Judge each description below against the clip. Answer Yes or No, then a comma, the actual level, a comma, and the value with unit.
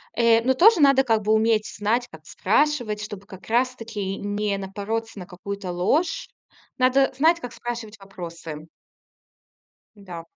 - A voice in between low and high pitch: No, high, 215 Hz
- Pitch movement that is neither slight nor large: Yes, average, 4.2 semitones